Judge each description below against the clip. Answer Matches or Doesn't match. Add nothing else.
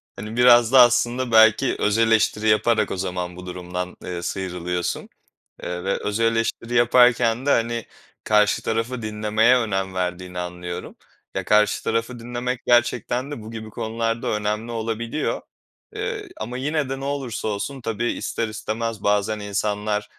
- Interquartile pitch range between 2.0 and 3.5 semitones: Matches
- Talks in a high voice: Doesn't match